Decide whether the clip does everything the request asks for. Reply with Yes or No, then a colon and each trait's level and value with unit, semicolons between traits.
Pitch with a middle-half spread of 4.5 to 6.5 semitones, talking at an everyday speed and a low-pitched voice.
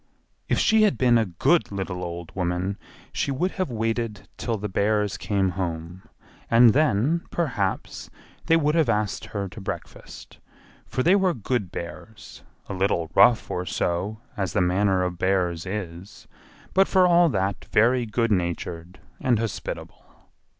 Yes: average, 5.1 semitones; average, 150 wpm; low, 105 Hz